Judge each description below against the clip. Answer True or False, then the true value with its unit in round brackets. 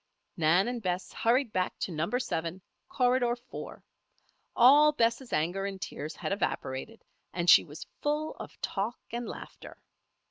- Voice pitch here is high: True (215 Hz)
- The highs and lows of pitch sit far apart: True (5.8 semitones)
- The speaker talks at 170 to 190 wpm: False (145 wpm)